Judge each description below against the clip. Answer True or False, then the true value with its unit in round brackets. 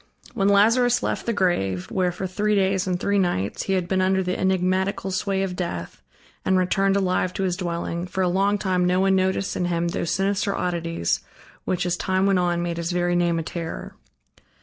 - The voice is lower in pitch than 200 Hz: True (185 Hz)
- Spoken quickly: True (210 wpm)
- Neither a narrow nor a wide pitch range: False (1.7 semitones)